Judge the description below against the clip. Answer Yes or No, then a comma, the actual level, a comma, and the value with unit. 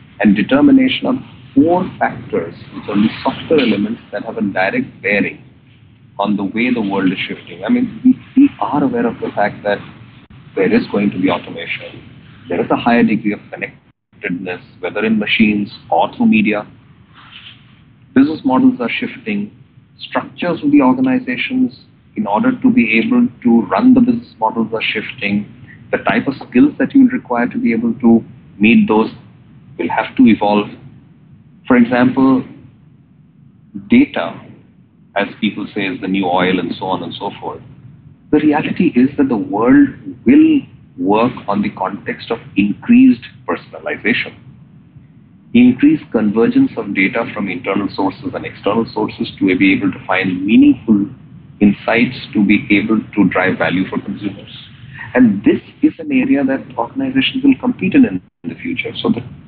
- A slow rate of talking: No, average, 160 wpm